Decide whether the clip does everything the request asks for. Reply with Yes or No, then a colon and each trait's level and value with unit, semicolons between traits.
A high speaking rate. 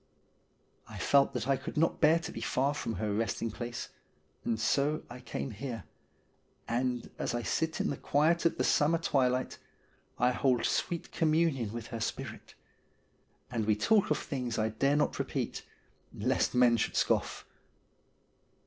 No: average, 160 wpm